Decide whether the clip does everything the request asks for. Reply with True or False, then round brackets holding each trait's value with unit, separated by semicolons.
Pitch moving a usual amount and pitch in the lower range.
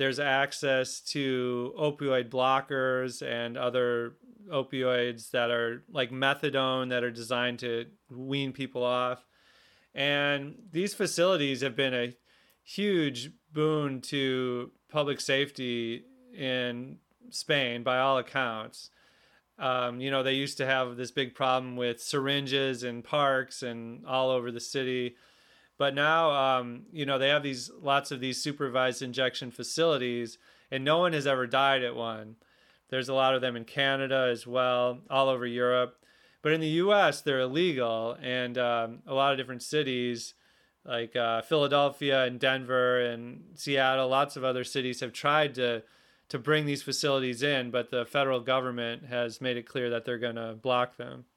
False (2.2 semitones; 130 Hz)